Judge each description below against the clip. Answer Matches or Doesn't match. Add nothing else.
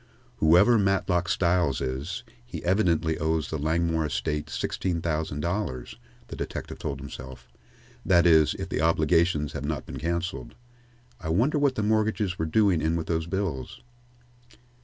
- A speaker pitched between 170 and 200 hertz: Doesn't match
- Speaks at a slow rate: Doesn't match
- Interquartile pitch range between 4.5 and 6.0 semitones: Doesn't match